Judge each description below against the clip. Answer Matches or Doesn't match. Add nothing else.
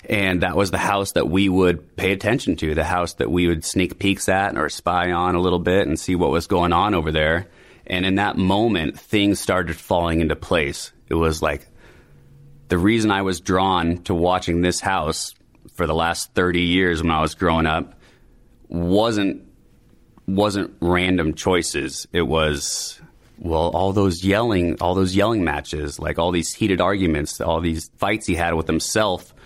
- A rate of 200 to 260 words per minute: Doesn't match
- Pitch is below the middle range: Matches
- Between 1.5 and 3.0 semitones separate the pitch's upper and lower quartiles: Matches